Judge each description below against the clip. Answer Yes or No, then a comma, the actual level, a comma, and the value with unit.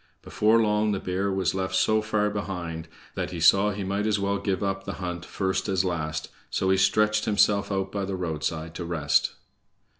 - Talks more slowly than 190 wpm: No, average, 200 wpm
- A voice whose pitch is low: Yes, very low, 95 Hz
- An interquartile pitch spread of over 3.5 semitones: No, average, 2.7 semitones